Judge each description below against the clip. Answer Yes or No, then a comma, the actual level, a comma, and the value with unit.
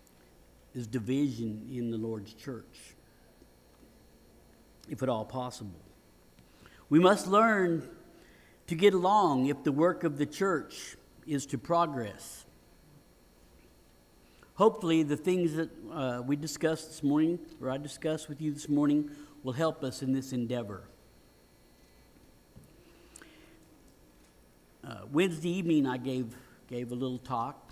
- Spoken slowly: Yes, slow, 120 wpm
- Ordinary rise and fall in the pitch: No, wide, 6.2 semitones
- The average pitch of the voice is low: Yes, low, 130 Hz